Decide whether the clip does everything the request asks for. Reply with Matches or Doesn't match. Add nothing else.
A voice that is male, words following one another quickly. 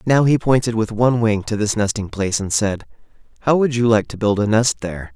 Matches